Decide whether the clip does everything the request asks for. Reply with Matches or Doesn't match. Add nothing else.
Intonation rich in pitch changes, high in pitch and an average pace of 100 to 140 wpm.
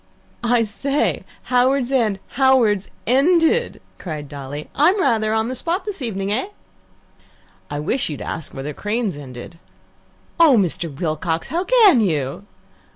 Matches